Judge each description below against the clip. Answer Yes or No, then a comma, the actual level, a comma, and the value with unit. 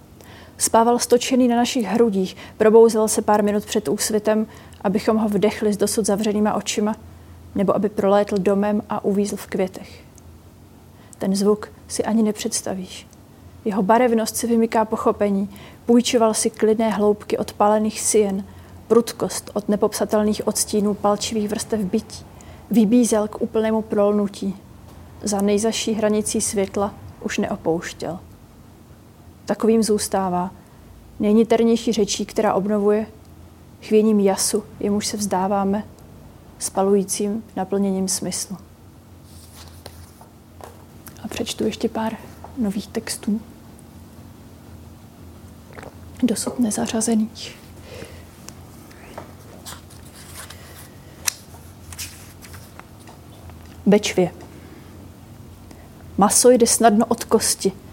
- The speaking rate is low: Yes, slow, 90 wpm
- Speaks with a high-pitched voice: Yes, high, 205 Hz